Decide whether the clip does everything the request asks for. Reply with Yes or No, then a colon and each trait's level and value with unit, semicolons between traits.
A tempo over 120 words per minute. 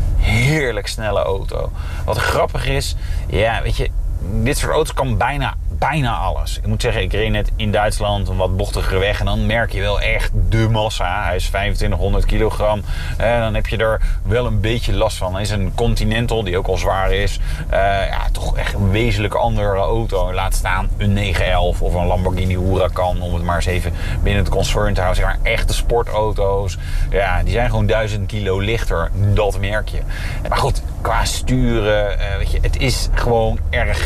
Yes: average, 195 wpm